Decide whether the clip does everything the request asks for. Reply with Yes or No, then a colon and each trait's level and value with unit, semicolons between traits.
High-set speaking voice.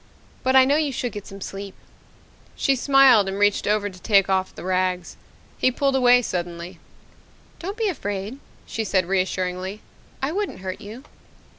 Yes: high, 205 Hz